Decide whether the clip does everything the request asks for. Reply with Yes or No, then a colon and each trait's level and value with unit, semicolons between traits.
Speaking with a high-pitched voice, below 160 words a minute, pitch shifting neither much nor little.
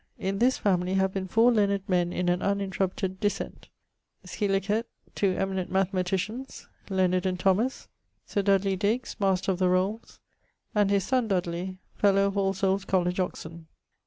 No: high, 195 Hz; average, 150 wpm; narrow, 1.5 semitones